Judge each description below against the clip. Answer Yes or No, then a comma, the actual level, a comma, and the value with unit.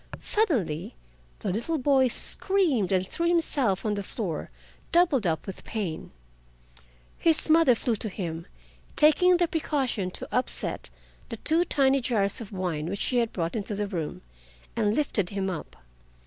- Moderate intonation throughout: No, wide, 7.8 semitones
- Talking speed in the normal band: Yes, average, 155 wpm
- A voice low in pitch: No, high, 225 Hz